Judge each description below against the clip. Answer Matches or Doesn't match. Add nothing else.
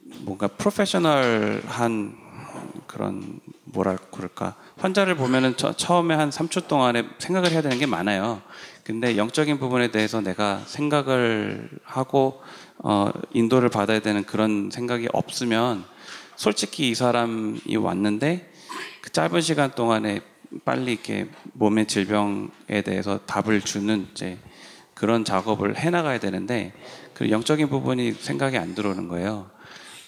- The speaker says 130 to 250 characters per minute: Doesn't match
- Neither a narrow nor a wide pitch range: Matches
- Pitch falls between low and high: Doesn't match